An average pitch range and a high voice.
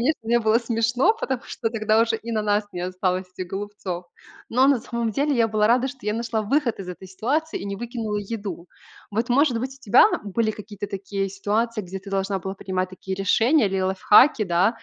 Yes: average, 3.4 semitones; high, 215 Hz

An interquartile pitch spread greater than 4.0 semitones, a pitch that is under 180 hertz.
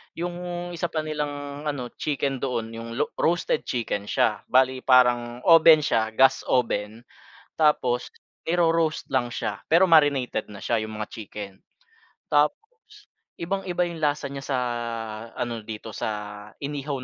Yes: average, 5.2 semitones; medium, 140 Hz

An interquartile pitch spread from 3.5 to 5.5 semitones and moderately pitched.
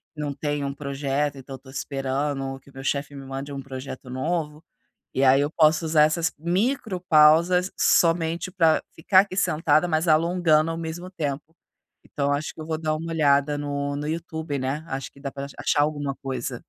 No: average, 2.7 semitones; medium, 150 Hz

